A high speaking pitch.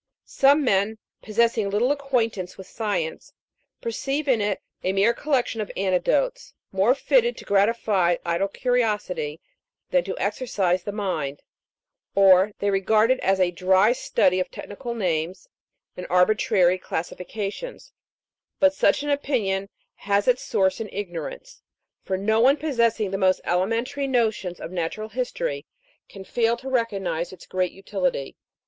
Yes: high, 210 Hz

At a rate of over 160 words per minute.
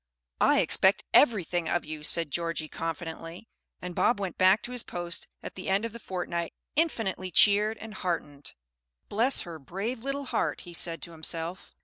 Yes: average, 170 wpm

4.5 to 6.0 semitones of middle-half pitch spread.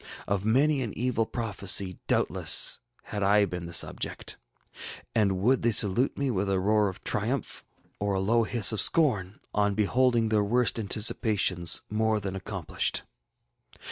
No: average, 3.0 semitones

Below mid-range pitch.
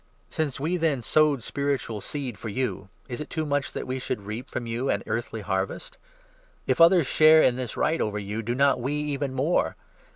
Yes: low, 130 Hz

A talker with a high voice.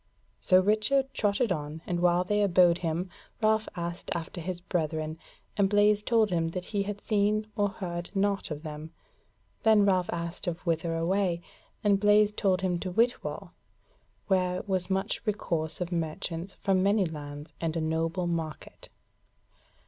No: medium, 180 Hz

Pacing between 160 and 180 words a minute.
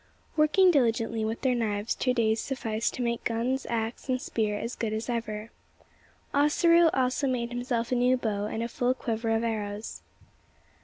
Yes: average, 170 wpm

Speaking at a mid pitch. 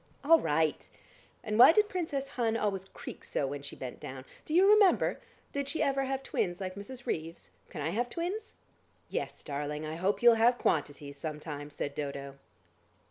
No: high, 195 Hz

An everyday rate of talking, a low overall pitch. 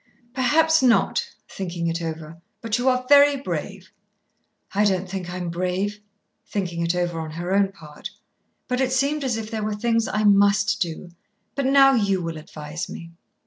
No: average, 175 wpm; high, 200 Hz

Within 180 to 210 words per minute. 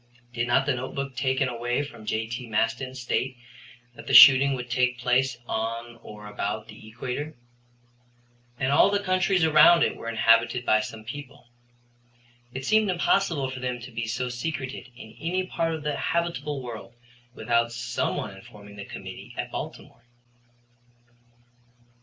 No: average, 155 wpm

